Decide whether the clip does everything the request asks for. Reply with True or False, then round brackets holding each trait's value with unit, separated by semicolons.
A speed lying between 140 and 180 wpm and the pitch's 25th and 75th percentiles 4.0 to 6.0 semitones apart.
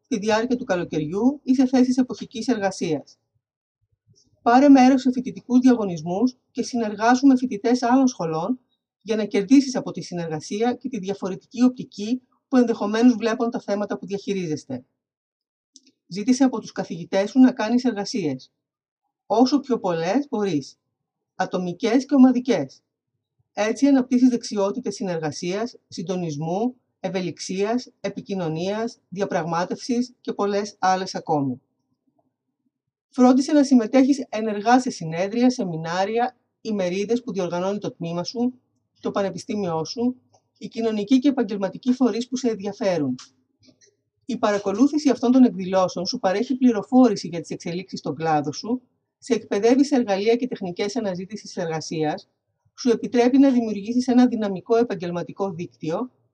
False (125 wpm; 5.1 semitones)